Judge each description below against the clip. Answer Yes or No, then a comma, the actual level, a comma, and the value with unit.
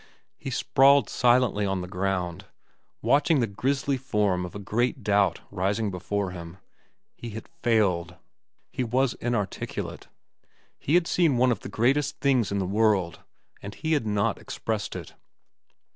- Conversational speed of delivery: Yes, average, 150 wpm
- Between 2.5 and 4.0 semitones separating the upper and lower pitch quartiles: No, average, 4.8 semitones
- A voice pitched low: Yes, low, 105 Hz